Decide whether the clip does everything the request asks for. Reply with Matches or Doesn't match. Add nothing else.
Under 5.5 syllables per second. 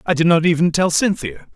Doesn't match